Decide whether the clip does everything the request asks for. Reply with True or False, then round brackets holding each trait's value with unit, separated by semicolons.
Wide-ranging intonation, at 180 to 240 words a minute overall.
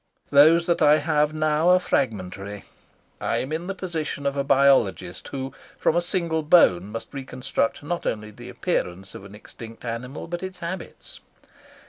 False (6.6 semitones; 165 wpm)